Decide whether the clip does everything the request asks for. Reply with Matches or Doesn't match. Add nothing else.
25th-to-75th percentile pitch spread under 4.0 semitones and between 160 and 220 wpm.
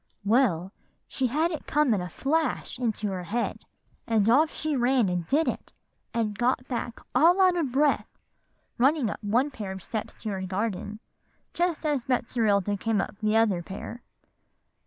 Doesn't match